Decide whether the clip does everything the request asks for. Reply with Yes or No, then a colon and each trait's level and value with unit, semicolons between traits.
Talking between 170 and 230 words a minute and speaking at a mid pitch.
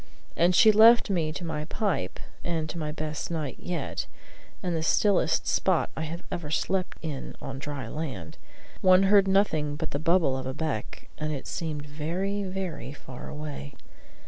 Yes: average, 175 wpm; medium, 160 Hz